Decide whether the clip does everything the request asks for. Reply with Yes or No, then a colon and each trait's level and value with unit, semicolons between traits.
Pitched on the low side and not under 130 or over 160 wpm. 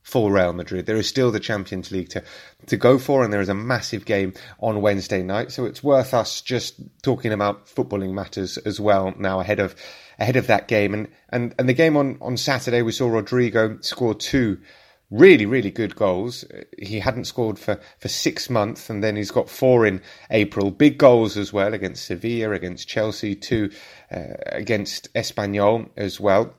No: low, 105 Hz; average, 190 wpm